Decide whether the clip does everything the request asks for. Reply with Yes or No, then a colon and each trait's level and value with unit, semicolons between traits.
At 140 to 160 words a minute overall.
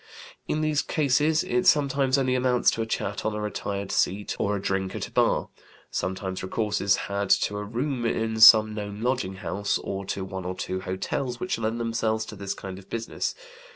No: average, 200 wpm